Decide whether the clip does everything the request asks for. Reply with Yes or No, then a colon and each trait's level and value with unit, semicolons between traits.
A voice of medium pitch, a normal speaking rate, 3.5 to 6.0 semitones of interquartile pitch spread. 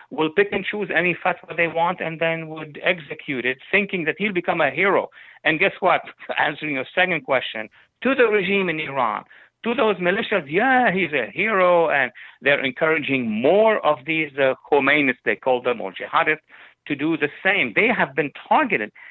Yes: medium, 165 Hz; average, 185 wpm; average, 4.5 semitones